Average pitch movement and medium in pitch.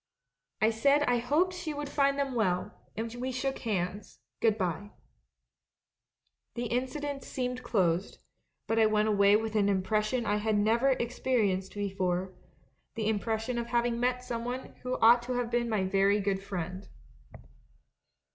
No: average, 3.6 semitones; high, 225 Hz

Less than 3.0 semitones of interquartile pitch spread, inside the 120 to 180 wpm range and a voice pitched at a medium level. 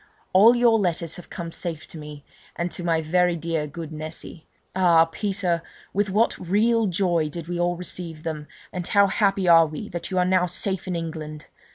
No: narrow, 2.6 semitones; average, 195 wpm; medium, 175 Hz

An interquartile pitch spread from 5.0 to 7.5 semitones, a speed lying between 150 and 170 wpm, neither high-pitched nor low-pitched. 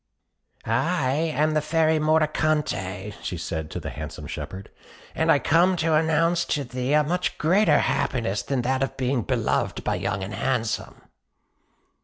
Yes: wide, 5.4 semitones; average, 155 wpm; medium, 145 Hz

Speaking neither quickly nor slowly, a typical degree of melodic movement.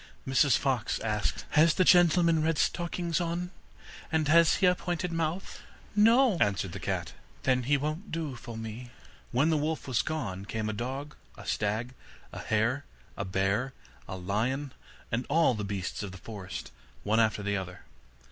No: average, 170 wpm; wide, 7.4 semitones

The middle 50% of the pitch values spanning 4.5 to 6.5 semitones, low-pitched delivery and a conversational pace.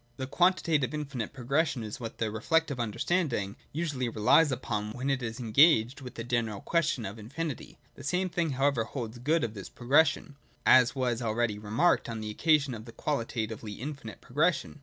Yes: average, 5.0 semitones; low, 125 Hz; average, 190 wpm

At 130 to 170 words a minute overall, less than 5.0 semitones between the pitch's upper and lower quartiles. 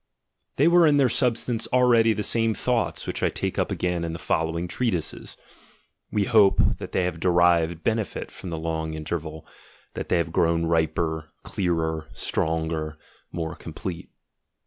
No: average, 165 wpm; wide, 5.5 semitones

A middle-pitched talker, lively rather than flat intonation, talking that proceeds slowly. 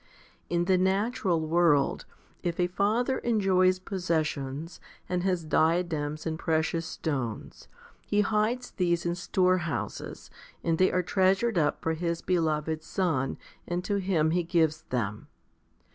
No: medium, 175 Hz; average, 2.8 semitones; slow, 130 wpm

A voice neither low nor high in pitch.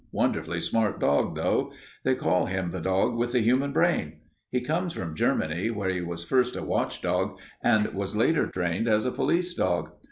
No: low, 105 Hz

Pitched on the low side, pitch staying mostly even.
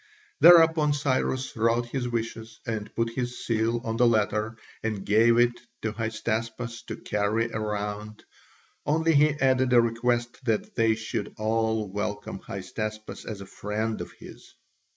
Yes: low, 115 Hz; narrow, 2.1 semitones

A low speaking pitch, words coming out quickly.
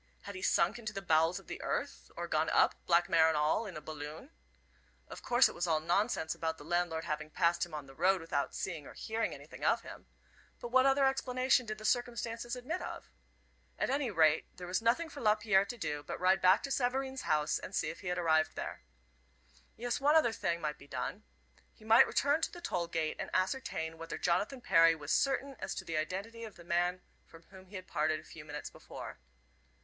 No: medium, 185 Hz; fast, 220 wpm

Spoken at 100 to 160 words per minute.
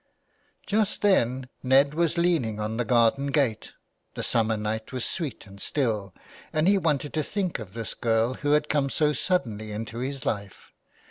No: average, 175 wpm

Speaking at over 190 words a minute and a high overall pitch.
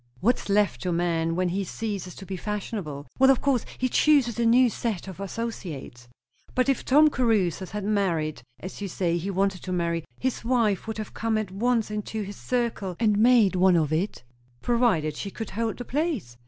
Yes: average, 200 wpm; high, 205 Hz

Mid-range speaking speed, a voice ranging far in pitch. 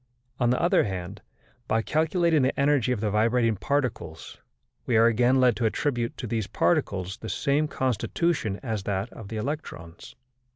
No: average, 165 wpm; average, 4.7 semitones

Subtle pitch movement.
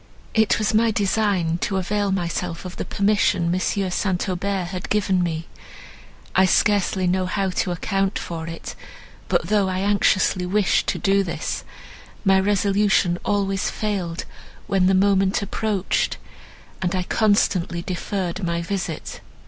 Yes: narrow, 2.1 semitones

